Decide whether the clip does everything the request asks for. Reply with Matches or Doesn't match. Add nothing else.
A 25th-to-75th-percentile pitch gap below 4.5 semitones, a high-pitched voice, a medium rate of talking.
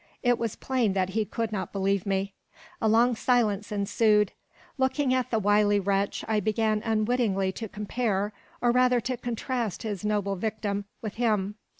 Matches